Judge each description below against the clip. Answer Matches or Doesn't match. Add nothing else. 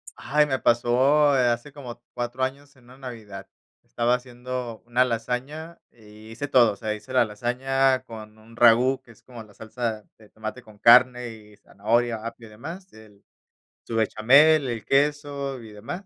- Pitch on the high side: Doesn't match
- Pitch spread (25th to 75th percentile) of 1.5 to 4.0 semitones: Matches